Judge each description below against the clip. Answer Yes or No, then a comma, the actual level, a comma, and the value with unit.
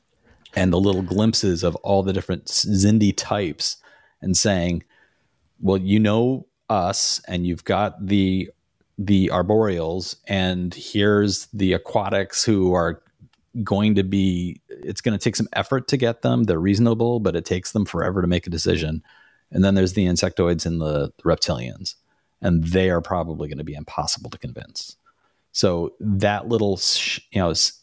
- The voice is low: Yes, very low, 95 Hz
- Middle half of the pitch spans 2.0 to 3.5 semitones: Yes, average, 2.8 semitones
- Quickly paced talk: No, average, 160 wpm